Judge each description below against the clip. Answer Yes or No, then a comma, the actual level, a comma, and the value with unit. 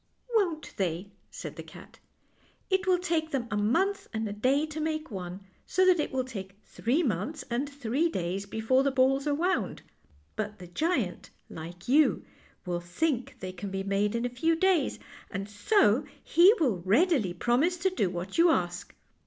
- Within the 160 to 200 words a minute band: Yes, average, 180 wpm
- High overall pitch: Yes, very high, 250 Hz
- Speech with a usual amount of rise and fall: No, wide, 8.4 semitones